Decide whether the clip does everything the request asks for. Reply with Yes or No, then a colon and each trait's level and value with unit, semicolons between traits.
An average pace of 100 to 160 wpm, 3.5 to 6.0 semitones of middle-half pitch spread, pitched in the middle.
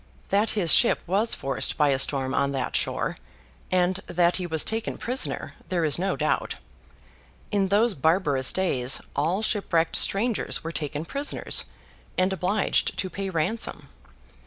Yes: average, 150 wpm; average, 4.6 semitones; medium, 180 Hz